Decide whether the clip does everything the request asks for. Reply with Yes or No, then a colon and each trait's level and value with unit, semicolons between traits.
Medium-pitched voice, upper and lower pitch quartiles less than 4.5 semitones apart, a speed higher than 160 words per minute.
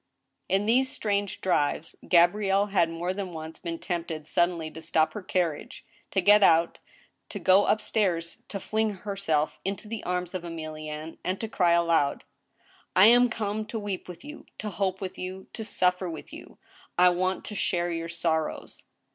Yes: medium, 180 Hz; average, 3.4 semitones; average, 180 wpm